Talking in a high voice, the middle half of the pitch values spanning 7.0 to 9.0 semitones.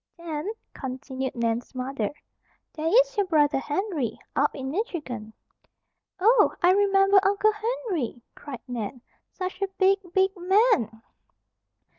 Yes: very high, 330 Hz; wide, 7.3 semitones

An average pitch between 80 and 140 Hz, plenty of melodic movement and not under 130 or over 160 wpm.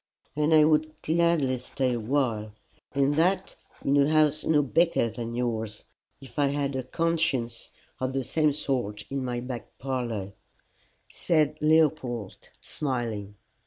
No: low, 135 Hz; average, 4.2 semitones; average, 140 wpm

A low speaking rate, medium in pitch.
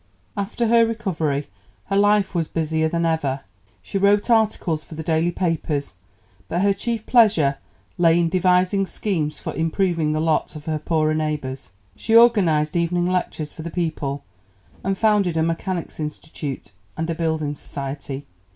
No: average, 155 wpm; medium, 165 Hz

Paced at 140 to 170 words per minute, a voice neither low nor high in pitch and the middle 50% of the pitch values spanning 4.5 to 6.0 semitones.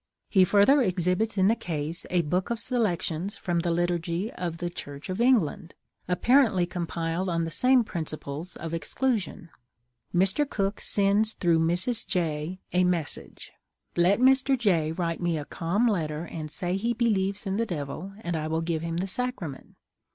No: average, 165 wpm; medium, 180 Hz; average, 3.9 semitones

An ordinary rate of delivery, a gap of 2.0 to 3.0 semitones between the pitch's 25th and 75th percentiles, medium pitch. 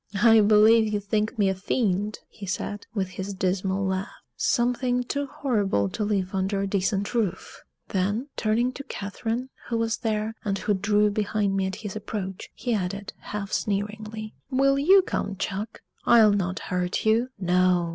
No: average, 165 wpm; narrow, 2.6 semitones; high, 210 Hz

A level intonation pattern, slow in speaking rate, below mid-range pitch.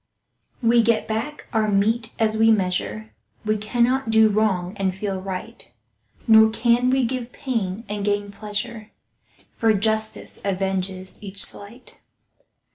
No: narrow, 2.3 semitones; slow, 130 wpm; high, 215 Hz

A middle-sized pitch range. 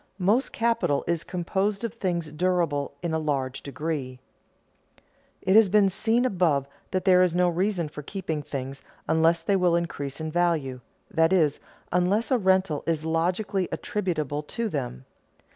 Yes: average, 4.1 semitones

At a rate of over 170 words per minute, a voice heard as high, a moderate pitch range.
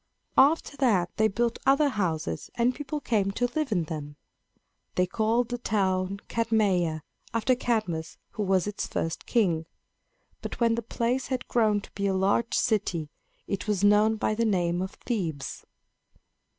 No: average, 160 wpm; high, 210 Hz; average, 4.3 semitones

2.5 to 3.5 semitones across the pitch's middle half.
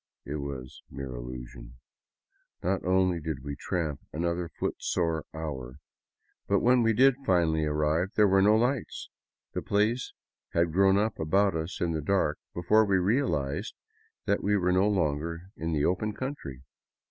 No: average, 5.0 semitones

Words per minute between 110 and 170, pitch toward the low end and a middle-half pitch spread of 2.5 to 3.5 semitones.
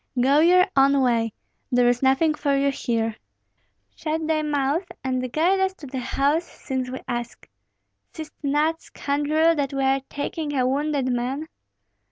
No: average, 160 wpm; very high, 280 Hz; average, 3.2 semitones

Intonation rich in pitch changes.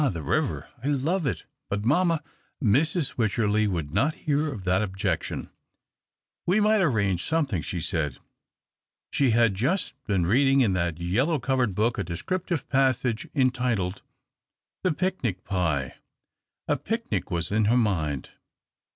Yes: wide, 7.6 semitones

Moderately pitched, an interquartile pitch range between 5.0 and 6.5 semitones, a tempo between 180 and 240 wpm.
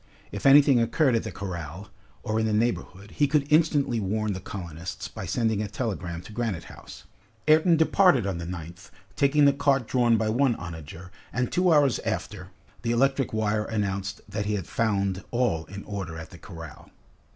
No: low, 110 Hz; average, 5.3 semitones; average, 190 wpm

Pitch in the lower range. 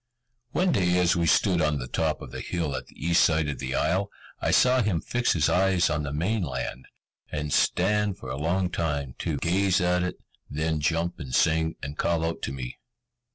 Yes: very low, 85 Hz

